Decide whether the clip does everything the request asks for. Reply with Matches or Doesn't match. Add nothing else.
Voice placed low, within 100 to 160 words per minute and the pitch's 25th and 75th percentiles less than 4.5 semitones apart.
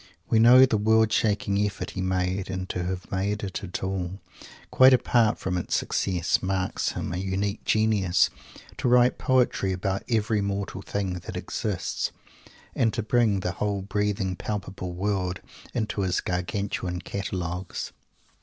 Matches